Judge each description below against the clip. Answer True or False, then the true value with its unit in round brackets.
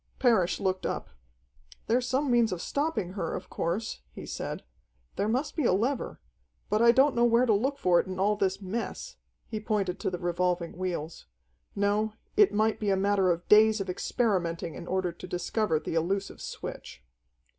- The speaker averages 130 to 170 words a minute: False (185 wpm)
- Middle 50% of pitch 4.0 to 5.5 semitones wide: True (4.3 semitones)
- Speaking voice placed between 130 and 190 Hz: False (200 Hz)